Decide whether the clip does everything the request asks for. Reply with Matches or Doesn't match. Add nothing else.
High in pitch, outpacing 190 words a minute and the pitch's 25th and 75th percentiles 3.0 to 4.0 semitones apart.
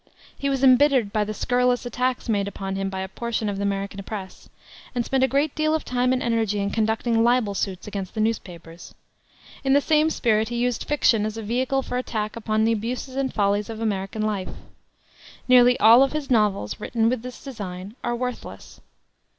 Matches